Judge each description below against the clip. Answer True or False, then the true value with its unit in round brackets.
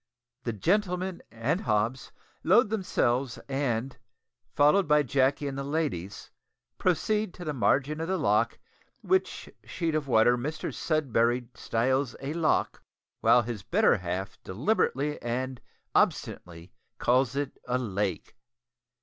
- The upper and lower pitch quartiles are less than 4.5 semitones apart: False (4.9 semitones)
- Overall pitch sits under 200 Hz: True (135 Hz)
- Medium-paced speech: False (125 wpm)